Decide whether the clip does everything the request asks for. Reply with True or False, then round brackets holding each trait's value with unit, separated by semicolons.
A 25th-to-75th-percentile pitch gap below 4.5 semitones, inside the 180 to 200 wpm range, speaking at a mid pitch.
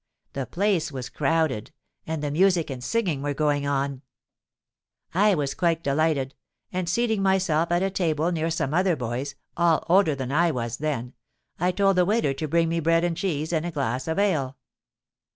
True (4.1 semitones; 185 wpm; 160 Hz)